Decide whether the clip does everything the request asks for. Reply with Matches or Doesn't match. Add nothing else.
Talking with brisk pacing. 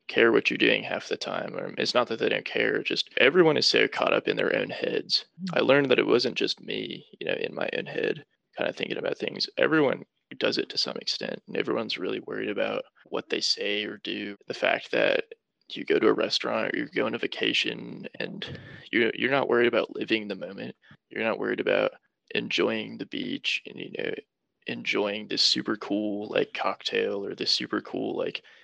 Matches